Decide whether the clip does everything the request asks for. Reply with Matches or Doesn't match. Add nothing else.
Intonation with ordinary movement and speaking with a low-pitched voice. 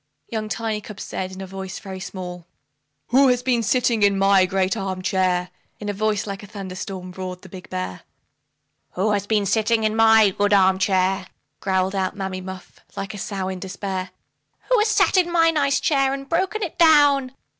Doesn't match